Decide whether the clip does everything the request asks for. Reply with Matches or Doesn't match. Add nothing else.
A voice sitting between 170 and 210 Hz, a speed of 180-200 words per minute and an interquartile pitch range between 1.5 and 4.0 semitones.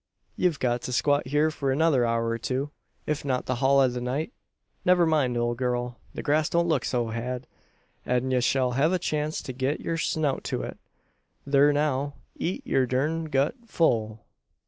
Doesn't match